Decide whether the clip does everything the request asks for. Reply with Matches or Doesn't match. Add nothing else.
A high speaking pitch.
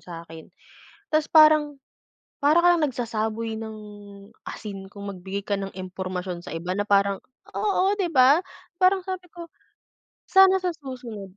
Matches